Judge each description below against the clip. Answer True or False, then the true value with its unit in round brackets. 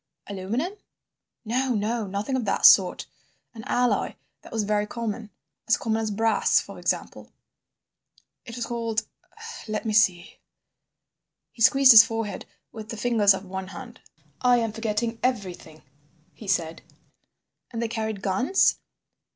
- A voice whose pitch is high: True (220 Hz)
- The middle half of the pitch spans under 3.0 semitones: True (2.5 semitones)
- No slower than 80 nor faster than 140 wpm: True (135 wpm)